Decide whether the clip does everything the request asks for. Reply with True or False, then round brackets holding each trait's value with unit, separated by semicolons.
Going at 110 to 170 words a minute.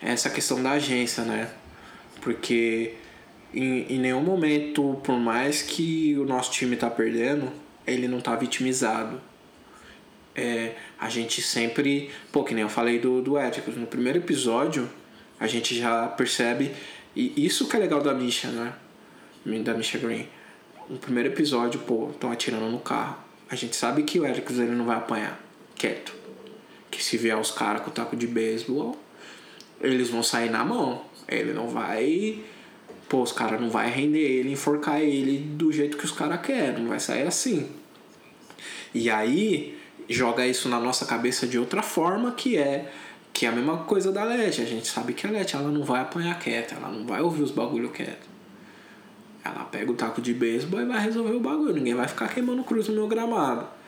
False (185 wpm)